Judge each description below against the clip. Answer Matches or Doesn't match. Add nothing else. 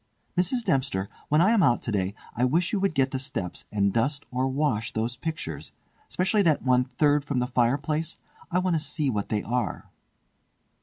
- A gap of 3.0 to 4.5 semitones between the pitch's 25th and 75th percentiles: Doesn't match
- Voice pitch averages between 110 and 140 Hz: Matches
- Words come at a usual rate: Matches